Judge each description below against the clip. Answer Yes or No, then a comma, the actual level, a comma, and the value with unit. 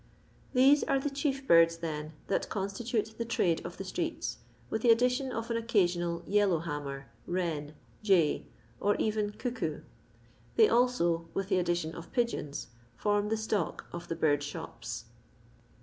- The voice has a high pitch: Yes, high, 195 Hz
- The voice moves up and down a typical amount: No, wide, 5.7 semitones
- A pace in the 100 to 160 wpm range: Yes, average, 150 wpm